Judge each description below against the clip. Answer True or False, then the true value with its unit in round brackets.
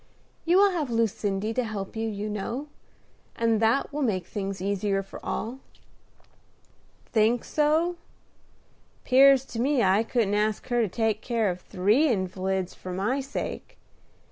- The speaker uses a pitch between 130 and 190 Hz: False (220 Hz)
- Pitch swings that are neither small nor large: True (4.5 semitones)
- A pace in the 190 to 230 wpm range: False (145 wpm)